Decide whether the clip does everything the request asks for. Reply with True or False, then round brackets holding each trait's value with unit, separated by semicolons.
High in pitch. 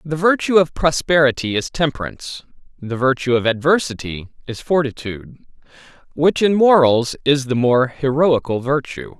False (140 Hz)